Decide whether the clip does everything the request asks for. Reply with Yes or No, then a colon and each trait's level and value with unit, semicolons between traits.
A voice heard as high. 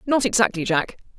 Yes: high, 205 Hz